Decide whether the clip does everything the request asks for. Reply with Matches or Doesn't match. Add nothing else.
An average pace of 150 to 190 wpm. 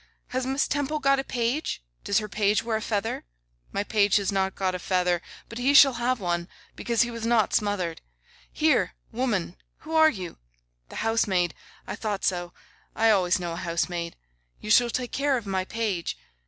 Matches